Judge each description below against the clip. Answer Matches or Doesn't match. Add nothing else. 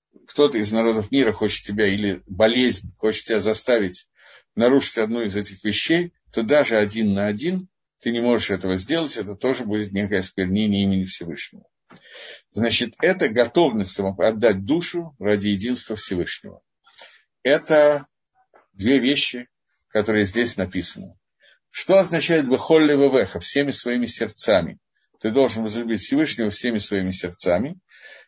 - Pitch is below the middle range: Matches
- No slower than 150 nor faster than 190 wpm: Doesn't match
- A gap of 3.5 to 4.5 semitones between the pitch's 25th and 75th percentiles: Doesn't match